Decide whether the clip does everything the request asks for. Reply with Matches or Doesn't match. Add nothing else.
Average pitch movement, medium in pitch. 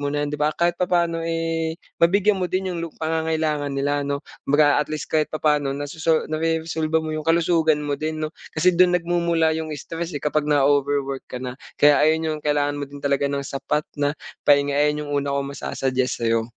Doesn't match